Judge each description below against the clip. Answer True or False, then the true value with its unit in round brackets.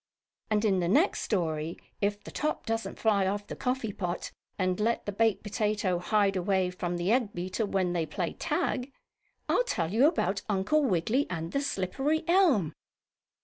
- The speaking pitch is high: True (205 Hz)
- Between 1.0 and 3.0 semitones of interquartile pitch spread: False (4.4 semitones)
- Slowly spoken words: False (175 wpm)